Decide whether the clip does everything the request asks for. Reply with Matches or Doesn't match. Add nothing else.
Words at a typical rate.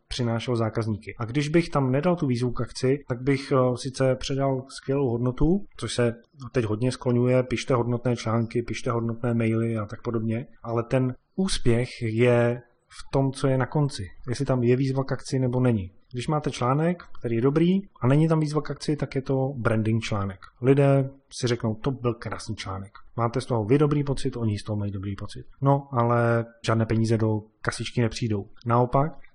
Doesn't match